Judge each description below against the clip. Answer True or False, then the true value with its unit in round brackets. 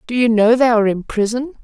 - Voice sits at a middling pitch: False (235 Hz)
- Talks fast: True (255 wpm)